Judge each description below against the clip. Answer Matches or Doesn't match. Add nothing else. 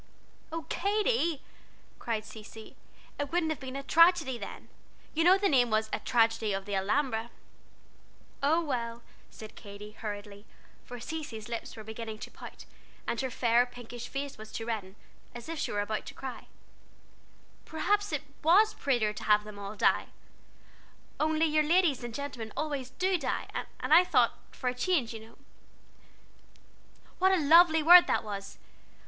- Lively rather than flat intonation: Matches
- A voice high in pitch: Matches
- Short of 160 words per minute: Matches